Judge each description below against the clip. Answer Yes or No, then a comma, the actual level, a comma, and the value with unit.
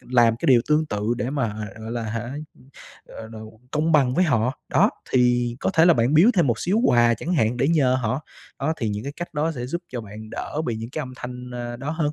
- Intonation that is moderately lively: Yes, average, 4.6 semitones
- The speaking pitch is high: No, low, 125 Hz